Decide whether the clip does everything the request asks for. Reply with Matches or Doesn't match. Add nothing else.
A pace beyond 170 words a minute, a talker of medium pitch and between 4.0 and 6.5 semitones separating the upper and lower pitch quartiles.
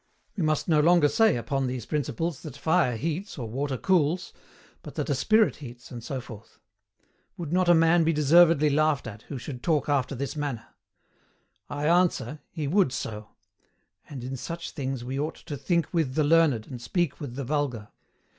Matches